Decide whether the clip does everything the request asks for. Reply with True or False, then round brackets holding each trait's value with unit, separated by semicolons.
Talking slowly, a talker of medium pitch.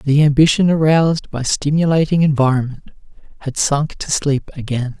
True (130 wpm; 145 Hz)